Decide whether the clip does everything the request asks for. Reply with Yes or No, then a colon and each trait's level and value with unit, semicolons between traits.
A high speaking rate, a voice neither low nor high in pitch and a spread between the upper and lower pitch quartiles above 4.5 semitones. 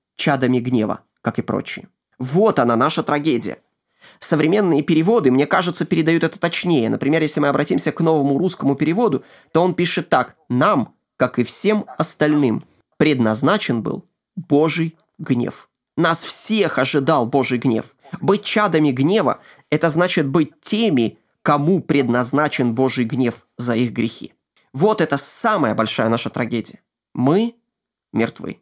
No: average, 135 wpm; medium, 150 Hz; average, 5.1 semitones